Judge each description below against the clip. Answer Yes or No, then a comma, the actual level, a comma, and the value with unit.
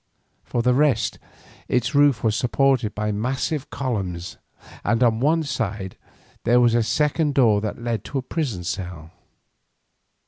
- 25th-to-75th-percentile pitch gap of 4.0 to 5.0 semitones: Yes, average, 4.4 semitones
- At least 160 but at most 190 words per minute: No, average, 145 wpm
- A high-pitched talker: No, low, 120 Hz